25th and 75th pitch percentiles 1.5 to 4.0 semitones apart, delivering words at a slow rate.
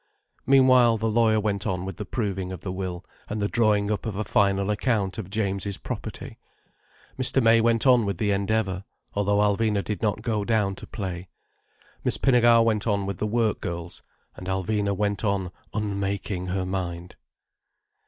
No: narrow, 2.4 semitones; average, 175 wpm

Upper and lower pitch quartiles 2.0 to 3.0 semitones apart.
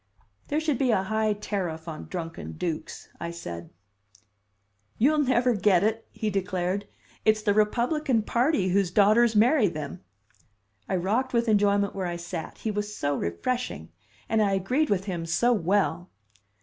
No: average, 4.8 semitones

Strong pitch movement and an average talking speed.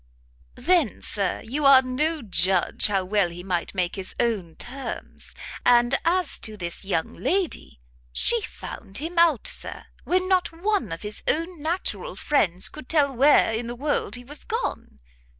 Yes: wide, 8.8 semitones; average, 165 wpm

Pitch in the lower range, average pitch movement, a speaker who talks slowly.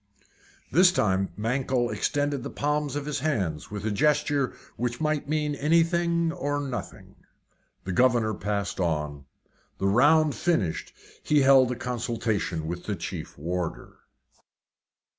No: low, 125 Hz; wide, 6.8 semitones; slow, 130 wpm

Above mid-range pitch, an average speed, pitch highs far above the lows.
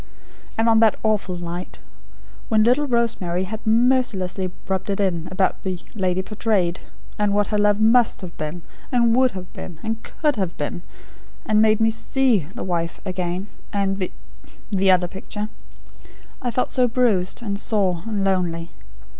No: high, 200 Hz; average, 170 wpm; average, 3.6 semitones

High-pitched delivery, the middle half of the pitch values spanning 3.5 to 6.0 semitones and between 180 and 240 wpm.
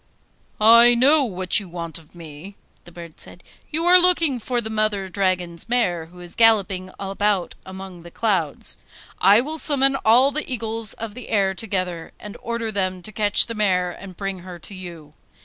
Yes: high, 200 Hz; average, 4.4 semitones; average, 185 wpm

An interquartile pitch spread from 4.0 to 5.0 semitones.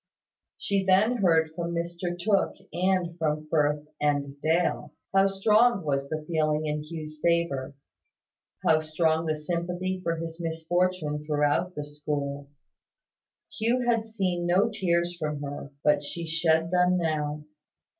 No: average, 3.2 semitones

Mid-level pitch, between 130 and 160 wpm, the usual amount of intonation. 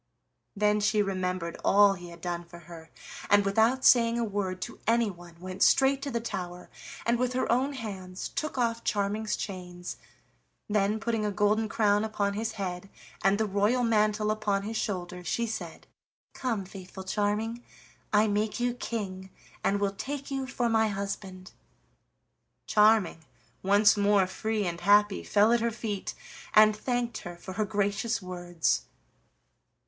No: high, 205 Hz; average, 155 wpm; average, 3.0 semitones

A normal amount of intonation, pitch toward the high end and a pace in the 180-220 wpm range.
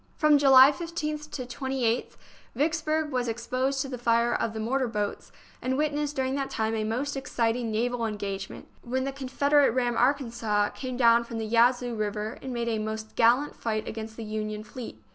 Yes: average, 3.4 semitones; high, 245 Hz; average, 190 wpm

